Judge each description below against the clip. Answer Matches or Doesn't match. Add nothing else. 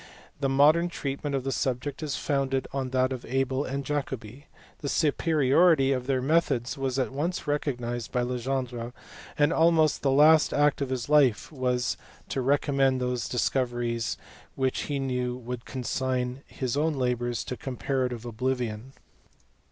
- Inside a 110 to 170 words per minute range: Matches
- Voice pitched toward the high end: Doesn't match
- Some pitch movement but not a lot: Doesn't match